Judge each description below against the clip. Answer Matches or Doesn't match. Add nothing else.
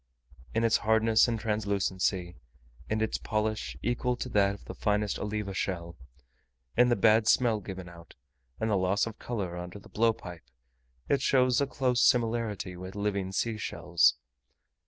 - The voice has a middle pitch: Doesn't match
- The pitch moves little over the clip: Doesn't match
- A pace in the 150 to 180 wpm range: Matches